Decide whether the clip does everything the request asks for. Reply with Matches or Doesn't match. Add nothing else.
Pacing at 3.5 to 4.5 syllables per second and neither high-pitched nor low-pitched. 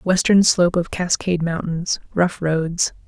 Matches